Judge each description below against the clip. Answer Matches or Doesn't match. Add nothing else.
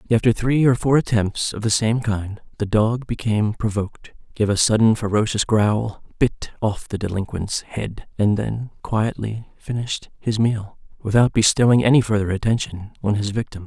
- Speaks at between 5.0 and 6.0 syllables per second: Doesn't match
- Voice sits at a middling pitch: Doesn't match